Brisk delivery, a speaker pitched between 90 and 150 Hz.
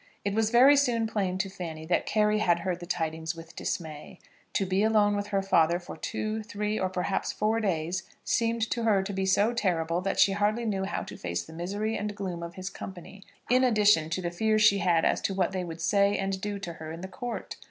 No: fast, 235 wpm; high, 195 Hz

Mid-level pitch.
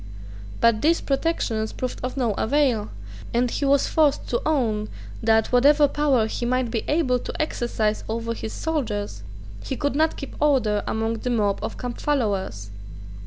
No: high, 245 Hz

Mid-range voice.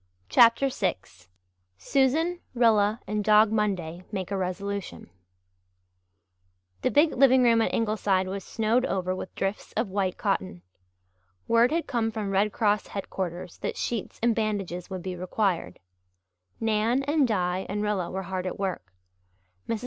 No: high, 205 Hz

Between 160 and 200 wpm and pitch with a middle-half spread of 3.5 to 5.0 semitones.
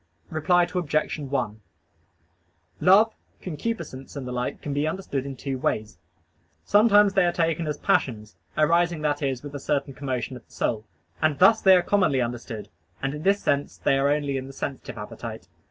Yes: average, 180 wpm; average, 4.7 semitones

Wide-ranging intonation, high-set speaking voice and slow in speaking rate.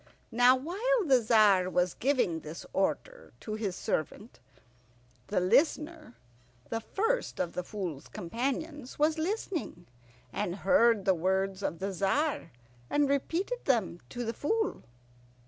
Yes: wide, 8.1 semitones; high, 235 Hz; slow, 130 wpm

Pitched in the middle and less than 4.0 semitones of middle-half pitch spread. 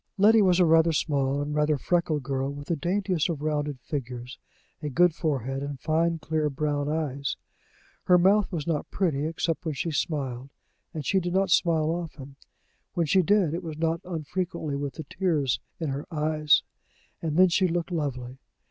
Yes: medium, 155 Hz; average, 3.3 semitones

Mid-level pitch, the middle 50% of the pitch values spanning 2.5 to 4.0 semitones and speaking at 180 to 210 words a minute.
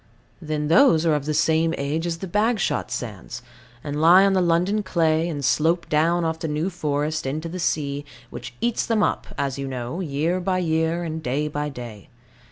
Yes: medium, 160 Hz; average, 3.1 semitones; average, 195 wpm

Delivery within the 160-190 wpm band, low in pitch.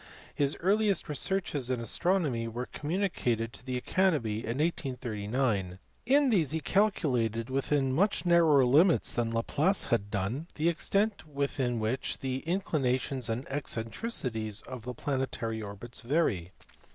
No: slow, 135 wpm; low, 130 Hz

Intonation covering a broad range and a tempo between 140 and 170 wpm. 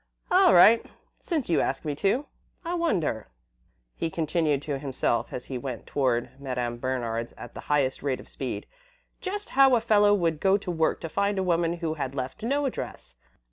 No: wide, 7.7 semitones; average, 185 wpm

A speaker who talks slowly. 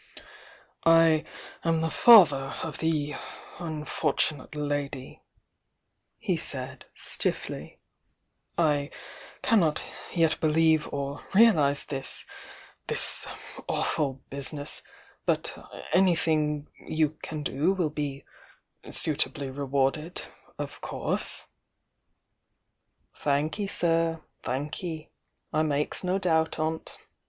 Yes: slow, 90 wpm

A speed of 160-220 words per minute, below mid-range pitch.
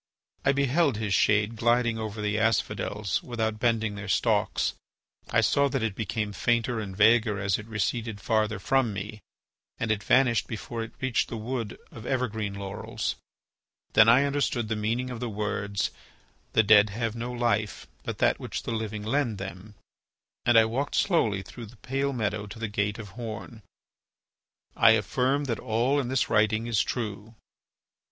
Yes: average, 170 wpm; low, 110 Hz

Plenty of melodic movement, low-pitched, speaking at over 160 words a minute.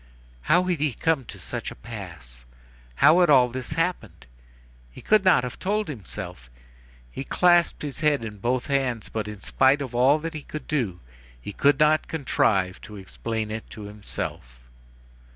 Yes: wide, 6.5 semitones; low, 130 Hz; average, 170 wpm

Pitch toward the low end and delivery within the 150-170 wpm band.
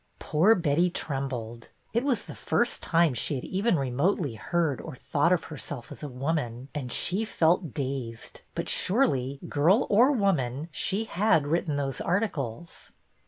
No: medium, 155 Hz; average, 155 wpm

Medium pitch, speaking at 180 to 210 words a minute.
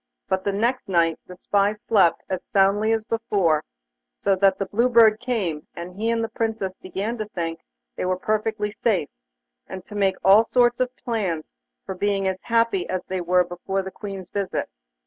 No: high, 200 Hz; average, 185 wpm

